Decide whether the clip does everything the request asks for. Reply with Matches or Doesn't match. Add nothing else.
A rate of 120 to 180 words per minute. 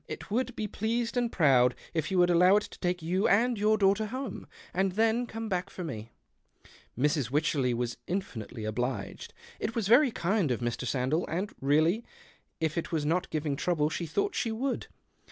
Doesn't match